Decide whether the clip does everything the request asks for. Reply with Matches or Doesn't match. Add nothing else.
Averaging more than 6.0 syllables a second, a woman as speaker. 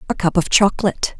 Matches